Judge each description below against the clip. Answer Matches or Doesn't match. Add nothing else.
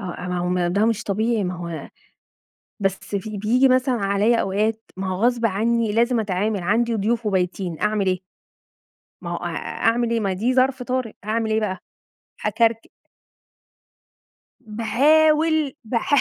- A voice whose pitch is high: Matches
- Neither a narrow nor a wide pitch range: Matches